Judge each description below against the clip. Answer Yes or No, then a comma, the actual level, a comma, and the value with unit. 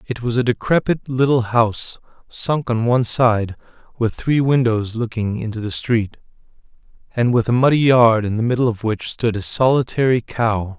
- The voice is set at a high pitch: No, low, 115 Hz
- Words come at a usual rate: Yes, average, 170 wpm